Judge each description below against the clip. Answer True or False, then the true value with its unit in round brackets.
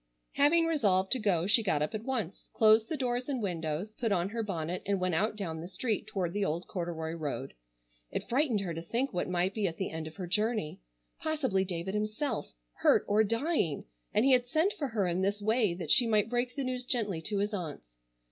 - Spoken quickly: True (225 wpm)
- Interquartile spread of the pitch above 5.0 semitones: True (5.5 semitones)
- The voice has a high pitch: True (205 Hz)